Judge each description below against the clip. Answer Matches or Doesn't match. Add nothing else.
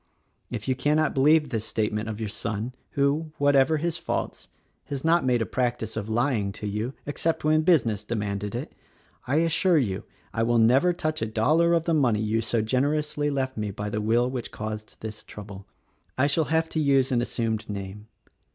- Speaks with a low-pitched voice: Matches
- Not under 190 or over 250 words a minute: Matches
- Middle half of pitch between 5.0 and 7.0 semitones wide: Matches